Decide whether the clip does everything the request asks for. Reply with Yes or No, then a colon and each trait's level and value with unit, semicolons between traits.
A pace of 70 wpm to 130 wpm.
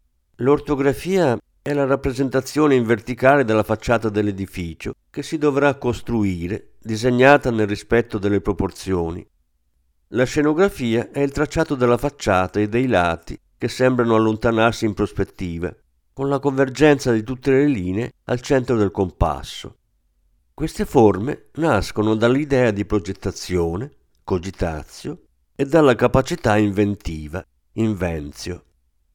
Yes: slow, 115 wpm